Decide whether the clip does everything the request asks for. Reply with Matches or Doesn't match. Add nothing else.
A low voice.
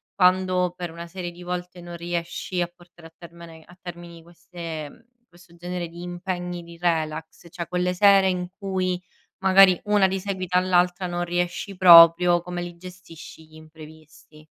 Doesn't match